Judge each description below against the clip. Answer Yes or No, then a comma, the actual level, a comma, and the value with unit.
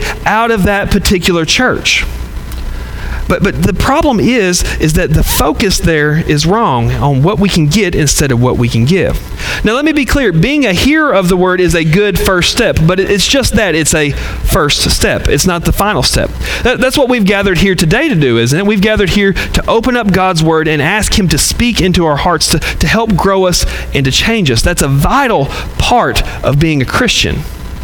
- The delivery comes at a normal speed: No, fast, 220 wpm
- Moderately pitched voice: Yes, medium, 180 Hz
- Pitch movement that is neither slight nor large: No, wide, 6.0 semitones